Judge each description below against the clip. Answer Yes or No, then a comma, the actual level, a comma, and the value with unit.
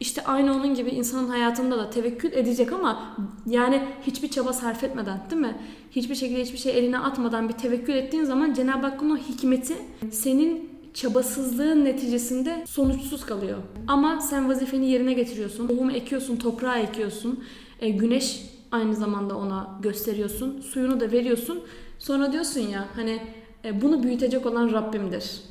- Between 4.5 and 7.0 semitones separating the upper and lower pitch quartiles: No, average, 2.8 semitones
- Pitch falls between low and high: No, very high, 250 Hz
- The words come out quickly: Yes, fast, 145 wpm